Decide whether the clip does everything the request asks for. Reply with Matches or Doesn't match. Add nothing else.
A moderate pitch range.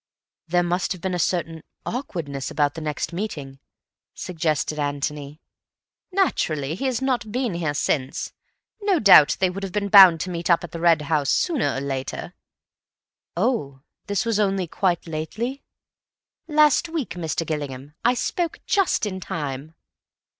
Doesn't match